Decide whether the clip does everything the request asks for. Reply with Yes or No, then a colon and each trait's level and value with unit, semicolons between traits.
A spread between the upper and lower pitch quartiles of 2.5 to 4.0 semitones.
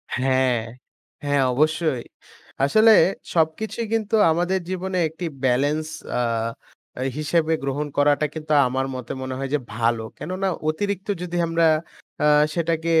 No: average, 4.4 semitones